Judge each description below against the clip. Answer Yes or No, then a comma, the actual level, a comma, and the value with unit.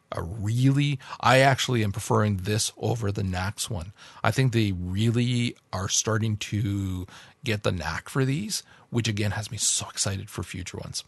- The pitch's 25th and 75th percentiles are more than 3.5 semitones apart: No, average, 3.1 semitones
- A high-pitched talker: No, low, 110 Hz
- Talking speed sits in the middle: Yes, average, 175 wpm